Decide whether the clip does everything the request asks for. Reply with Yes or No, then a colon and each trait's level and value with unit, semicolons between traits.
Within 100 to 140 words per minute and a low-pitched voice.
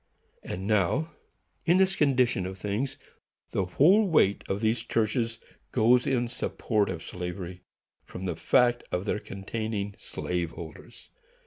Yes: slow, 135 wpm; low, 110 Hz